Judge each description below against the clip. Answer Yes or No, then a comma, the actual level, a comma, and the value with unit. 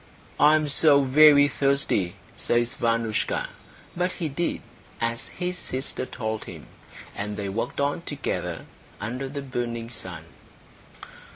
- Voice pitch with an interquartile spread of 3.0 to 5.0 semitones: Yes, average, 3.9 semitones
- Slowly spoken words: Yes, slow, 125 wpm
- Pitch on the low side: Yes, low, 130 Hz